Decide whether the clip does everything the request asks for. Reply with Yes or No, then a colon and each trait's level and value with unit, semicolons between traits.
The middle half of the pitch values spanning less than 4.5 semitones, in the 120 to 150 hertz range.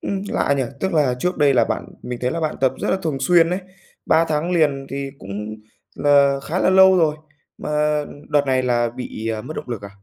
No: average, 4.8 semitones; medium, 140 Hz